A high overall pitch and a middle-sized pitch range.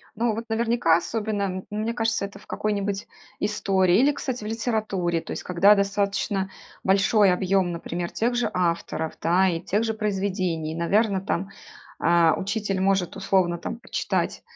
Yes: high, 195 Hz; average, 3.3 semitones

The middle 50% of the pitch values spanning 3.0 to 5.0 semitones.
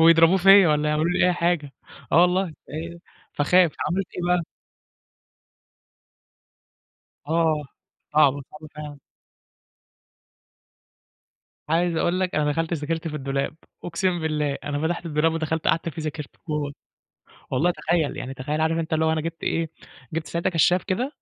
No: narrow, 2.4 semitones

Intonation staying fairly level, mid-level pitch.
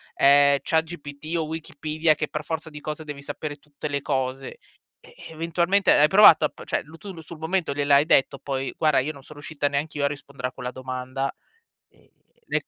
Yes: narrow, 2.2 semitones; medium, 150 Hz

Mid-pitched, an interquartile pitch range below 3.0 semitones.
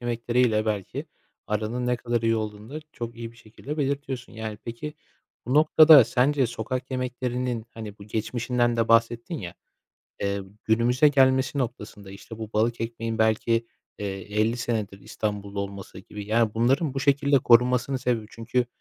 No: low, 115 Hz; narrow, 2.6 semitones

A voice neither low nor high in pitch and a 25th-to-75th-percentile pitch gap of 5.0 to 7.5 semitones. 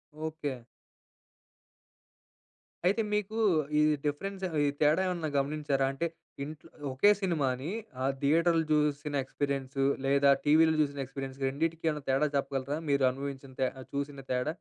No: medium, 145 Hz; narrow, 2.5 semitones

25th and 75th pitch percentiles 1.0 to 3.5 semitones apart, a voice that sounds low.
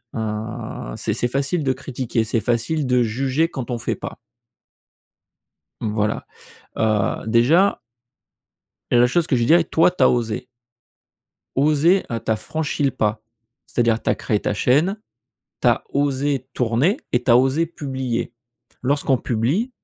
No: average, 4.1 semitones; low, 125 Hz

